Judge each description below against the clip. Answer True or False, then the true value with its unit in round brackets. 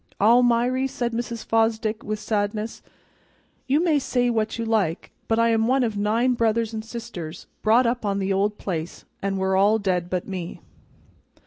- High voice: True (220 Hz)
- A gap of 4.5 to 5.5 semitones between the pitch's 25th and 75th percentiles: False (2.8 semitones)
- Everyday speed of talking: True (175 wpm)